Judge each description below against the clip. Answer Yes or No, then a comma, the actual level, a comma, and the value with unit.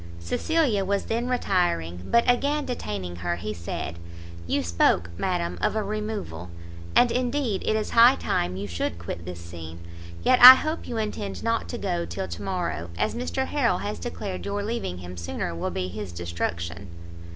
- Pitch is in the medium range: No, low, 105 Hz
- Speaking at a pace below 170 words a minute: No, average, 175 wpm